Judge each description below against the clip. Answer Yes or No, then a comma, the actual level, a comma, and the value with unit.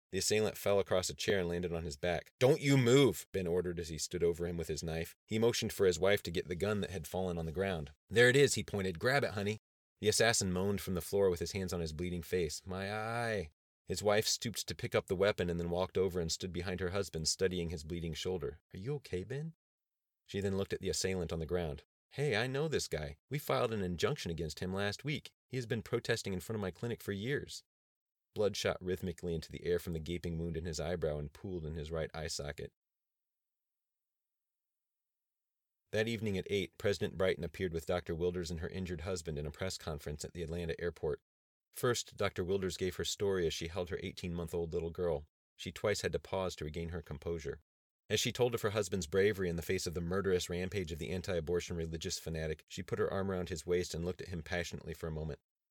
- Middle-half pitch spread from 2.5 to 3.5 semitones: Yes, average, 2.9 semitones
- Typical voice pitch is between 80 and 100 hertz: Yes, very low, 90 Hz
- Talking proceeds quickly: Yes, fast, 240 wpm